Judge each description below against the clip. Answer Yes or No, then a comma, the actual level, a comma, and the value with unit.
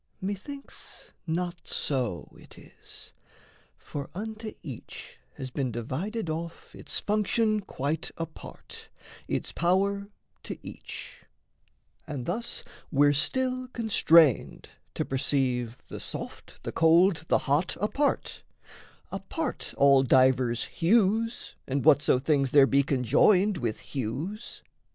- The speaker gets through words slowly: Yes, slow, 110 wpm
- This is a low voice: No, medium, 160 Hz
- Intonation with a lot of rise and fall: Yes, wide, 7.2 semitones